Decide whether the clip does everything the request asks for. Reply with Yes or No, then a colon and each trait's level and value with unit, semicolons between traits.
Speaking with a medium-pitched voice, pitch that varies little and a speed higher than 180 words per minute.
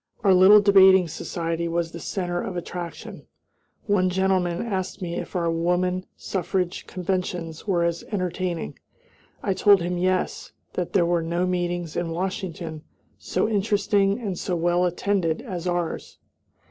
No: medium, 180 Hz; narrow, 1.9 semitones; average, 145 wpm